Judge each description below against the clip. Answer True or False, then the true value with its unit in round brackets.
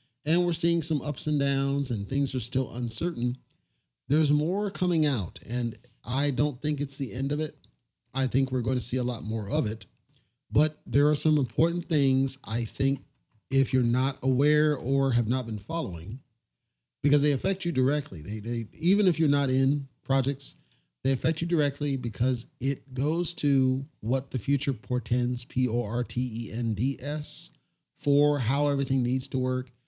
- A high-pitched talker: False (135 Hz)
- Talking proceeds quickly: False (170 wpm)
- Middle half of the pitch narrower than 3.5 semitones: True (3.1 semitones)